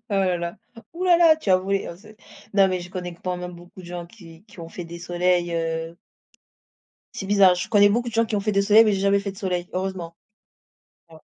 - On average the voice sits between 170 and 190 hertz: Yes, medium, 185 Hz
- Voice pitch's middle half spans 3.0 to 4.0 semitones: No, narrow, 2.6 semitones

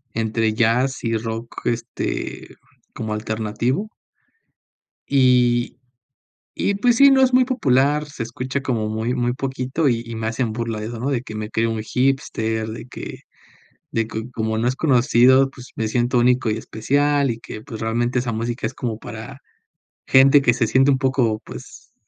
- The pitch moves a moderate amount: Yes, average, 3.0 semitones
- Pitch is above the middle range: No, low, 120 Hz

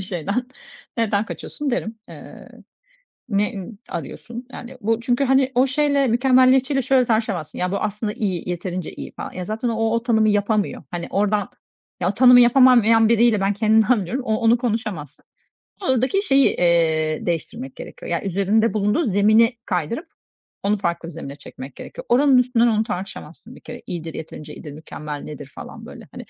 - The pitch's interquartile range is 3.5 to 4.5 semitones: No, average, 5.1 semitones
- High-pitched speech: Yes, high, 220 Hz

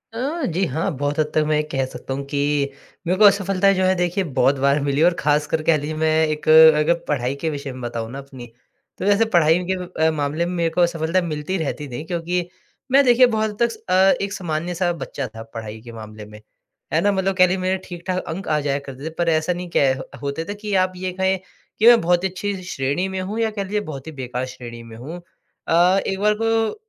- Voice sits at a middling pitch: Yes, medium, 170 Hz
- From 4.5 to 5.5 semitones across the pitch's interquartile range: Yes, average, 4.8 semitones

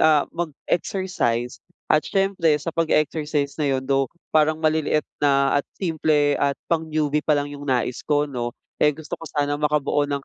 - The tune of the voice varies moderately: No, narrow, 1.8 semitones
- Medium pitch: Yes, medium, 150 Hz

